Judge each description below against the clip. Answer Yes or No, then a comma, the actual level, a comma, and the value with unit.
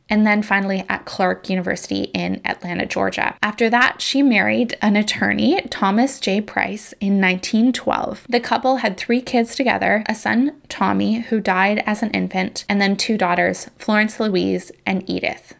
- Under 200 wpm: Yes, average, 160 wpm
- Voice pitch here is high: Yes, high, 215 Hz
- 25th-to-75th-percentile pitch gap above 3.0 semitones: Yes, average, 3.8 semitones